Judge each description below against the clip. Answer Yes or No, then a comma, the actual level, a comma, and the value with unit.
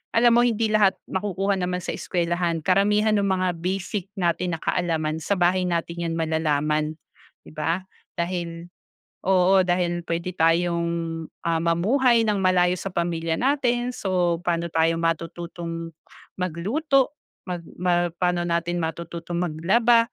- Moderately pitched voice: Yes, medium, 175 Hz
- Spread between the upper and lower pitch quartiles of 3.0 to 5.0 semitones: No, narrow, 2.5 semitones